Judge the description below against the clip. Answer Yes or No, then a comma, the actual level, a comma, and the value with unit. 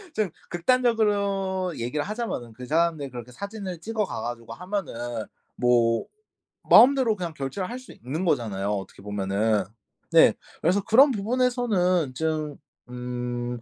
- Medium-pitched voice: Yes, medium, 165 Hz